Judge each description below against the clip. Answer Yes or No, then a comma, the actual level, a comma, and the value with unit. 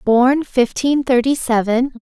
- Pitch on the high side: Yes, very high, 250 Hz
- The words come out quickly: No, slow, 120 wpm